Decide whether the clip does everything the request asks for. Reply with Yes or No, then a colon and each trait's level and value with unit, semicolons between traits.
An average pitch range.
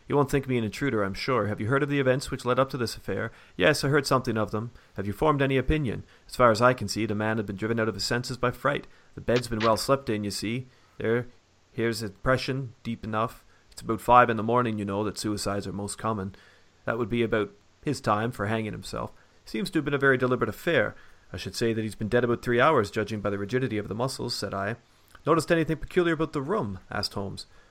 Yes: average, 3.6 semitones